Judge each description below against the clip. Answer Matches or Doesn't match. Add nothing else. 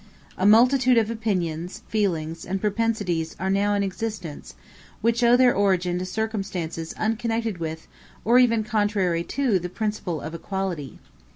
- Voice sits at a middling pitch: Doesn't match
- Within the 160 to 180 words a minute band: Doesn't match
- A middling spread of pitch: Matches